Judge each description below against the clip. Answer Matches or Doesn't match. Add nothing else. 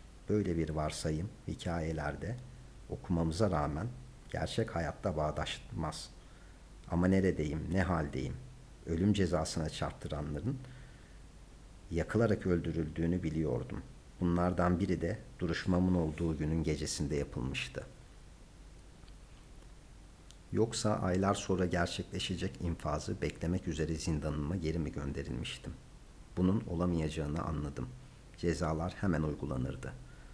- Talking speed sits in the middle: Doesn't match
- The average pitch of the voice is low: Matches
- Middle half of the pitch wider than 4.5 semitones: Doesn't match